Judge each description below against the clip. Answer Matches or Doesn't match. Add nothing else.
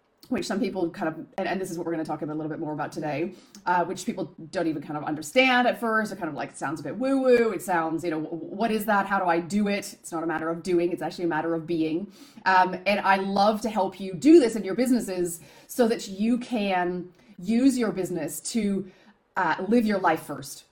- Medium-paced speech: Doesn't match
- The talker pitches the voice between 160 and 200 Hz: Matches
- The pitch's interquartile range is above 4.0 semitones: Matches